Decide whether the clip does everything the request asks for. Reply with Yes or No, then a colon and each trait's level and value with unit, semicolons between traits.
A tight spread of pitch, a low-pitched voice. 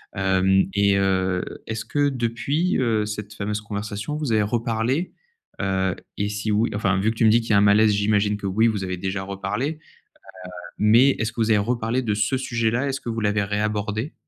Yes: narrow, 2.3 semitones; low, 105 Hz